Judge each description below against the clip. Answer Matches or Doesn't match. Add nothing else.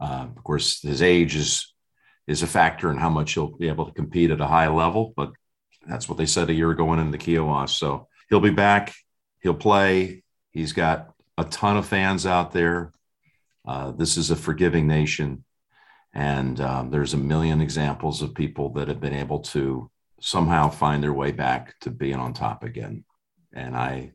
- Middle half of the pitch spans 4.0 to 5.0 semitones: Doesn't match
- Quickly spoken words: Doesn't match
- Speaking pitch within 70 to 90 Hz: Matches